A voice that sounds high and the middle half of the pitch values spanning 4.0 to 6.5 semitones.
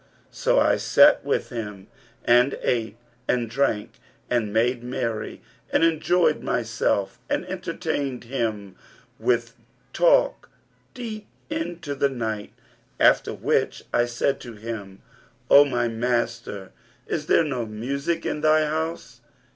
No: low, 125 Hz; average, 5.0 semitones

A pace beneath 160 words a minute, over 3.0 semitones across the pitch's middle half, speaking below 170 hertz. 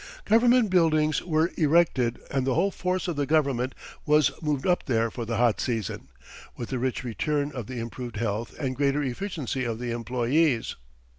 No: average, 175 wpm; average, 4.7 semitones; low, 135 Hz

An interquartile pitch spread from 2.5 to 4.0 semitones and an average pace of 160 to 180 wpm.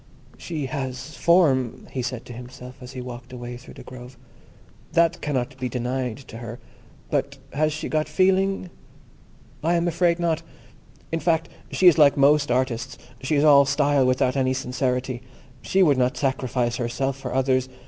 Yes: average, 3.5 semitones; average, 165 wpm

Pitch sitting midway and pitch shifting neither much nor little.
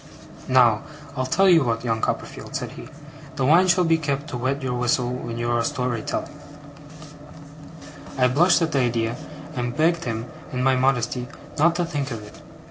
No: low, 130 Hz; average, 4.1 semitones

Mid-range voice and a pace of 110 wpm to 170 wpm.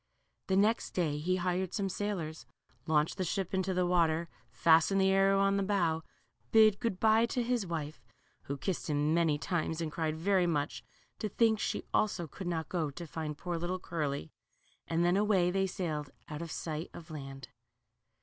No: medium, 175 Hz; average, 185 wpm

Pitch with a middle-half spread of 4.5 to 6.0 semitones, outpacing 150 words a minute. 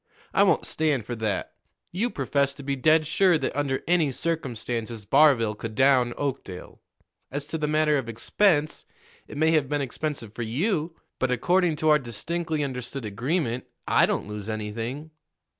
Yes: average, 4.8 semitones; average, 165 wpm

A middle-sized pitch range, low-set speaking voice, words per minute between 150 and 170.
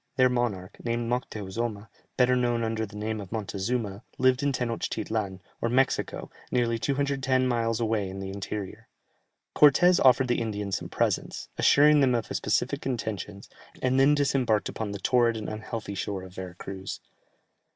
Yes: average, 3.8 semitones; low, 115 Hz; average, 160 wpm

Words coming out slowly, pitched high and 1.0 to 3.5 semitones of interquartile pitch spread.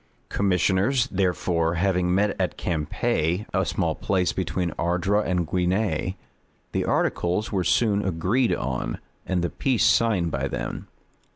No: slow, 130 wpm; very low, 90 Hz; average, 2.8 semitones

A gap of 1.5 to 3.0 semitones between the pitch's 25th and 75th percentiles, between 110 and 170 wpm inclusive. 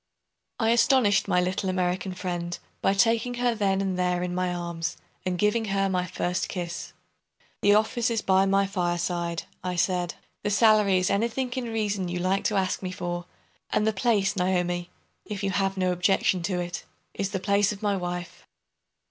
No: narrow, 2.5 semitones; average, 180 wpm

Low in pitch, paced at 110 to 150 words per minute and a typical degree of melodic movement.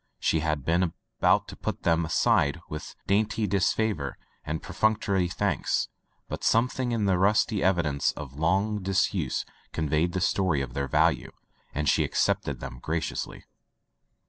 Yes: very low, 90 Hz; average, 145 wpm; average, 4.6 semitones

